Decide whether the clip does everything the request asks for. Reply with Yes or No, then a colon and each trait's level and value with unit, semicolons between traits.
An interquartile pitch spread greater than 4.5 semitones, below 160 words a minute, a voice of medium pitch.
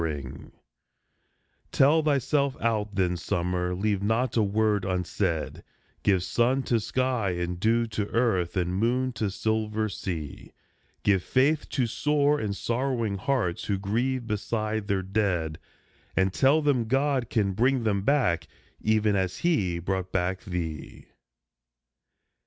No: average, 5.0 semitones; average, 140 wpm; low, 105 Hz